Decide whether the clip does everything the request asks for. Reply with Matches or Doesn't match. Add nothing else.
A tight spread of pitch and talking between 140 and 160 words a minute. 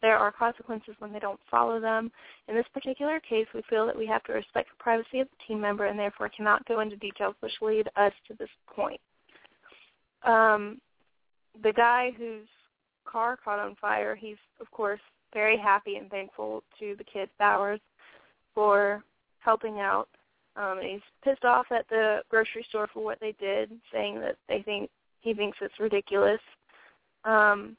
Doesn't match